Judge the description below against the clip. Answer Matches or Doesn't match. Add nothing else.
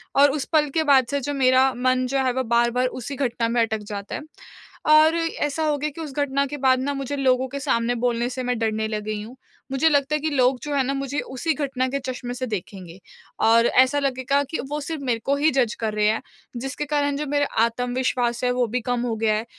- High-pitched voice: Matches